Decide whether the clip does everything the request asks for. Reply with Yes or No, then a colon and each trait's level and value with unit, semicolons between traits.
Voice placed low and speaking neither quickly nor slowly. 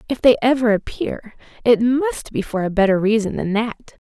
No: high, 230 Hz; average, 190 wpm